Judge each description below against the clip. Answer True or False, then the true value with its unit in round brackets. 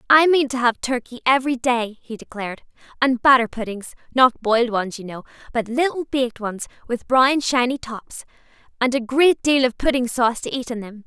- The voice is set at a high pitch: True (245 Hz)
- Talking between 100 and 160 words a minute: False (195 wpm)